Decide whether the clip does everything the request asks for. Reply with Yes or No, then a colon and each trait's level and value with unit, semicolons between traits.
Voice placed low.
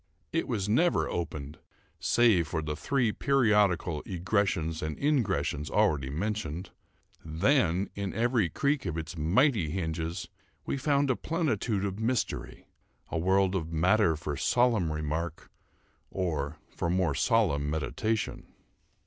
Yes: very low, 95 Hz